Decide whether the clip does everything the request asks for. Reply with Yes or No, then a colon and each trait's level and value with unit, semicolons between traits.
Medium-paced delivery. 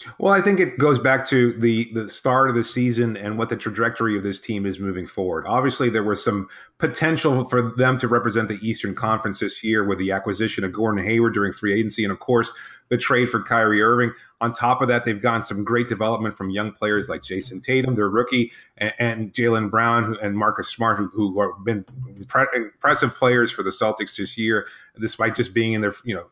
No: fast, 220 wpm